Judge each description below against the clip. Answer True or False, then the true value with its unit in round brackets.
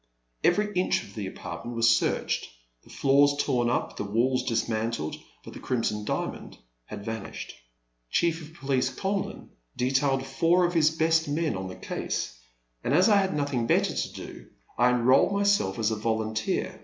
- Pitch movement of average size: False (6.1 semitones)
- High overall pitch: False (130 Hz)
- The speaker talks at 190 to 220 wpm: False (175 wpm)